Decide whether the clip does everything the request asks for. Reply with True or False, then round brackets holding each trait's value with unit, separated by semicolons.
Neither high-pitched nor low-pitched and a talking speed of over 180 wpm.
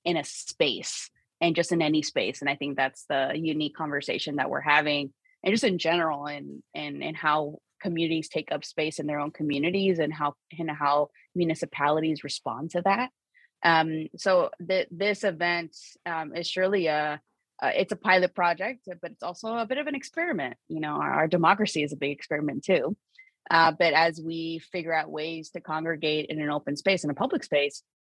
True (160 Hz; 200 wpm)